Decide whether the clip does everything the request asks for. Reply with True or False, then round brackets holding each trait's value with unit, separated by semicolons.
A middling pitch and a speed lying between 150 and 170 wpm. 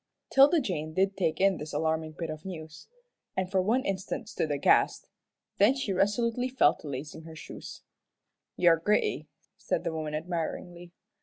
True (175 Hz; 165 wpm)